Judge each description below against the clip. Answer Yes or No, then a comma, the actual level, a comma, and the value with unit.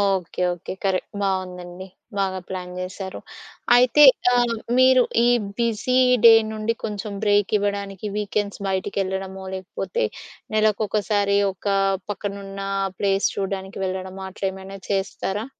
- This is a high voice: Yes, high, 195 Hz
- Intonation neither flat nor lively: No, narrow, 1.8 semitones